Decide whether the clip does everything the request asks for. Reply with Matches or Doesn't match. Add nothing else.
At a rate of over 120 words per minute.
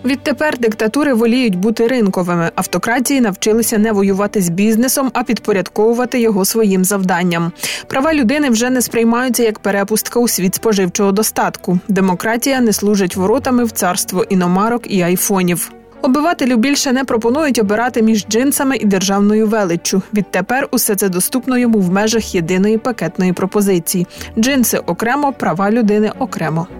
Matches